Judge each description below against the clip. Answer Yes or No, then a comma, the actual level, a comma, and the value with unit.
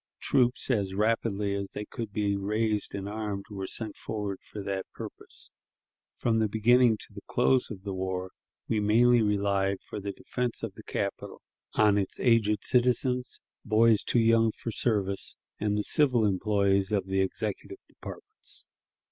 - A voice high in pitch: No, low, 105 Hz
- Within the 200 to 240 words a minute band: No, average, 160 wpm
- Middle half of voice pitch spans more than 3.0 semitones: No, narrow, 2.5 semitones